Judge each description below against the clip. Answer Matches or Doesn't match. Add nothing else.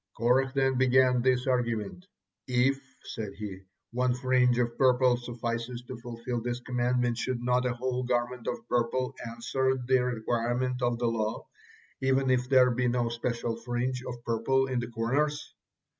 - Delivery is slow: Doesn't match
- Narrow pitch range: Matches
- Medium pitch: Doesn't match